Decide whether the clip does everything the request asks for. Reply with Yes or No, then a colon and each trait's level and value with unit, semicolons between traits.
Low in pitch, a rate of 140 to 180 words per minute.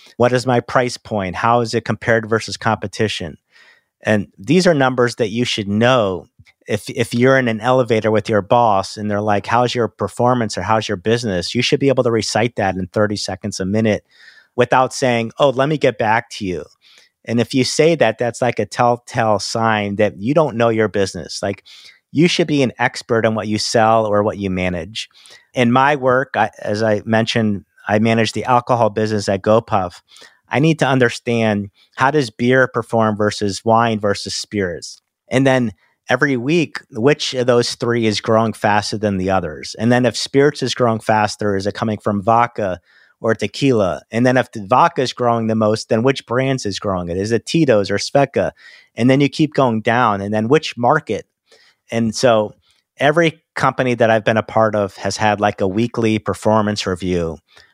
No: low, 115 Hz; average, 195 wpm